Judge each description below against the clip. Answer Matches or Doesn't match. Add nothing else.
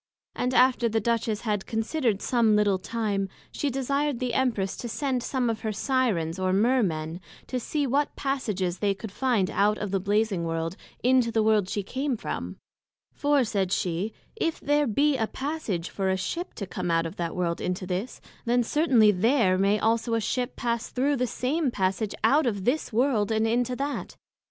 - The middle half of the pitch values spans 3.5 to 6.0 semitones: Matches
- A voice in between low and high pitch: Doesn't match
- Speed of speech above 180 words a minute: Matches